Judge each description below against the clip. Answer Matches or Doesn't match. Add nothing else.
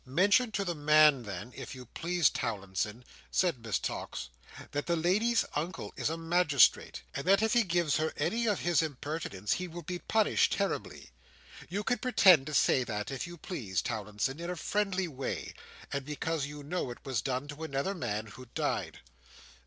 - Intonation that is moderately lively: Doesn't match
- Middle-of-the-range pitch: Matches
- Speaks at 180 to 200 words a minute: Matches